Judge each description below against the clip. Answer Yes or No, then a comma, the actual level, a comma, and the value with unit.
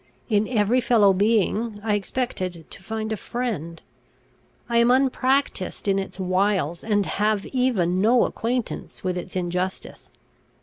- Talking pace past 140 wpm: No, slow, 135 wpm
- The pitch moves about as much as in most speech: Yes, average, 4.1 semitones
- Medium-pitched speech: No, high, 210 Hz